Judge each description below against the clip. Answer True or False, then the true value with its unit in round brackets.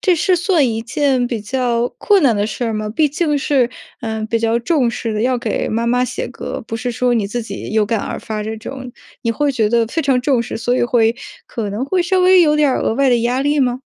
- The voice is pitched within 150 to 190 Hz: False (245 Hz)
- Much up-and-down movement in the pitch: False (3.8 semitones)